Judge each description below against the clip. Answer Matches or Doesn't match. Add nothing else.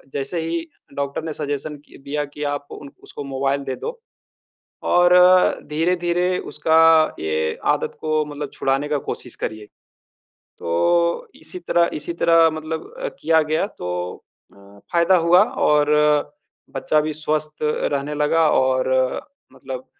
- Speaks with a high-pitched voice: Doesn't match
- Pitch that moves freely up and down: Doesn't match